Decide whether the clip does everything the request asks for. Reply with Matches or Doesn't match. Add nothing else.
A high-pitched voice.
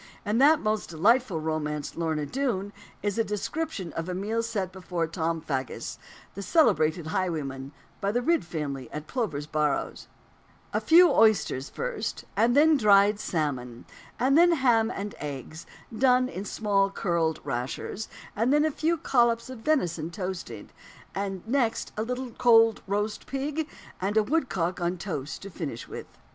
Matches